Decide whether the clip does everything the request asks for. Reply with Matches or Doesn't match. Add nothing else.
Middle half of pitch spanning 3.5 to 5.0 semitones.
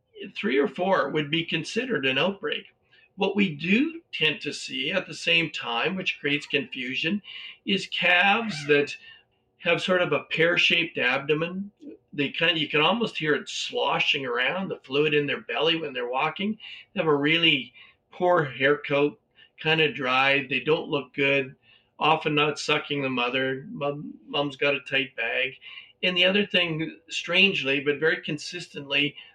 Matches